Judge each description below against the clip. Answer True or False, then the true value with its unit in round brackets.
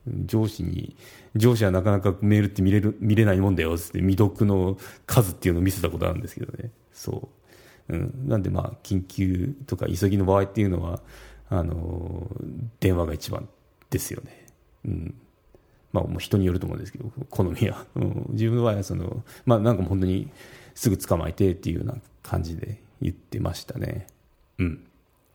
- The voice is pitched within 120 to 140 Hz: False (100 Hz)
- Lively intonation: False (4.3 semitones)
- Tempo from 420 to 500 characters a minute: False (355 characters per minute)